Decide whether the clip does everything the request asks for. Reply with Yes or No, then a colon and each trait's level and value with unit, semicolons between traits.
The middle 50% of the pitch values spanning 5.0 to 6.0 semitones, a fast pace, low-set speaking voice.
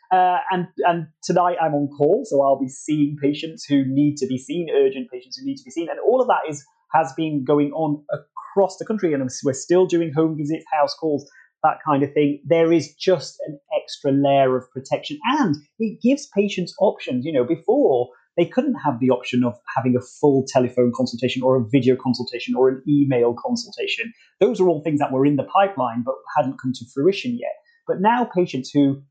No: wide, 5.5 semitones; fast, 210 wpm; medium, 150 Hz